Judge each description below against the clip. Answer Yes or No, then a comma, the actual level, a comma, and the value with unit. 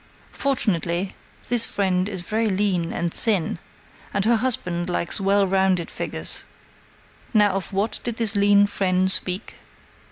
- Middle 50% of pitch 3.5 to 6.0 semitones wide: No, narrow, 2.5 semitones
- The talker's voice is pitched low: No, high, 195 Hz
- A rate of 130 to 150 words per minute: Yes, slow, 135 wpm